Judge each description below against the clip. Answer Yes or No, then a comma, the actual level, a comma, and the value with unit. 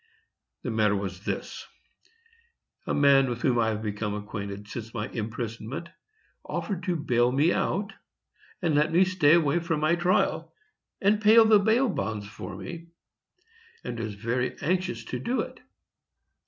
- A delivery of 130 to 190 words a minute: Yes, average, 155 wpm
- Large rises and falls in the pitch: Yes, wide, 8.0 semitones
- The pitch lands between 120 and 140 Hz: Yes, low, 135 Hz